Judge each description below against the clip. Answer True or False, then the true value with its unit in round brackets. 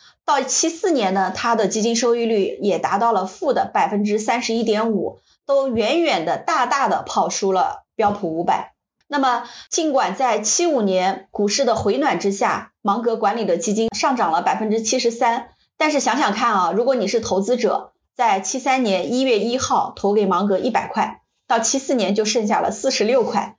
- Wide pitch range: False (4.4 semitones)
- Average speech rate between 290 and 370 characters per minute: False (280 characters per minute)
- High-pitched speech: True (230 Hz)